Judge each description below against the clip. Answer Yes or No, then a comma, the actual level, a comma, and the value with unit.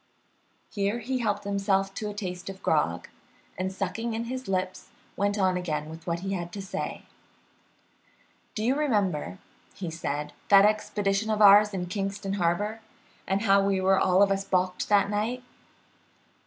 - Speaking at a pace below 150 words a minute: No, average, 165 wpm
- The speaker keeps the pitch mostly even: Yes, narrow, 2.1 semitones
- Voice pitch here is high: Yes, high, 195 Hz